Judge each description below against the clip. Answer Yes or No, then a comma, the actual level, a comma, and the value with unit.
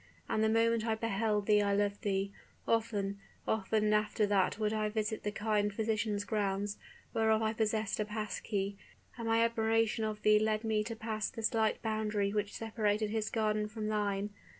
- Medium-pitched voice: No, high, 215 Hz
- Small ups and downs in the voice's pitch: Yes, narrow, 1.2 semitones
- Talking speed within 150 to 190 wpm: Yes, average, 175 wpm